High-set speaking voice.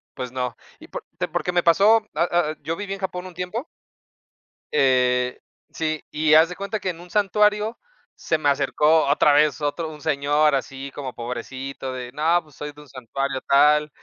No: medium, 150 Hz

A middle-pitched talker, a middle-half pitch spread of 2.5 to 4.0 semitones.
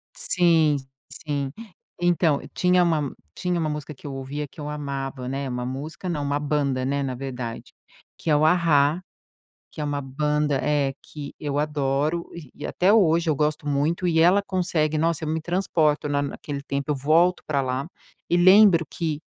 Yes: medium, 150 Hz; average, 2.9 semitones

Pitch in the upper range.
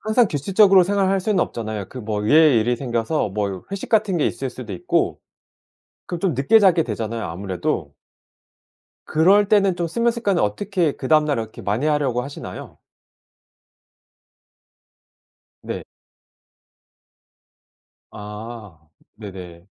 No: medium, 140 Hz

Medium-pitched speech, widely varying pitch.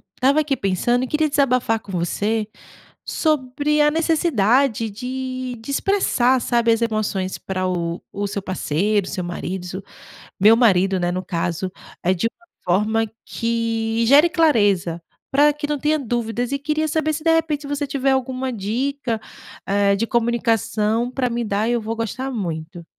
No: high, 230 Hz; wide, 5.7 semitones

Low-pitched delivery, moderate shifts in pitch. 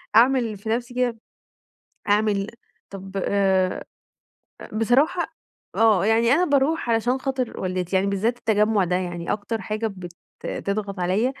No: high, 215 Hz; average, 3.9 semitones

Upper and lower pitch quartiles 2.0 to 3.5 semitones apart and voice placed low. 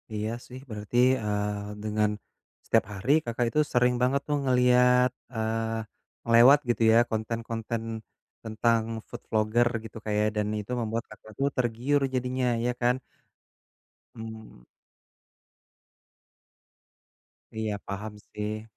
Yes: narrow, 2.5 semitones; low, 115 Hz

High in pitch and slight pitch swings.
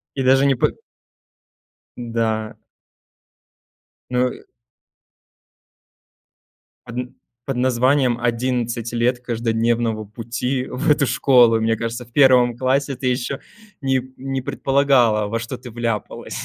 No: low, 125 Hz; narrow, 2.1 semitones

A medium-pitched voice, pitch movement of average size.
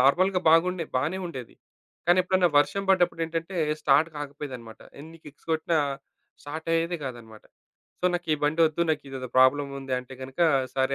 Yes: medium, 155 Hz; average, 4.1 semitones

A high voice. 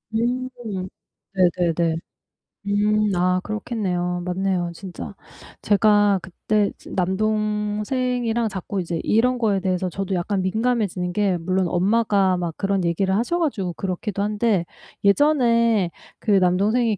Yes: high, 200 Hz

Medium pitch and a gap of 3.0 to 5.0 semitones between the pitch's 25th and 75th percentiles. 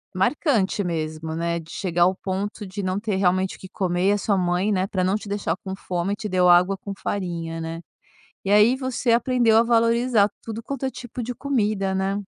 No: high, 195 Hz; average, 3.6 semitones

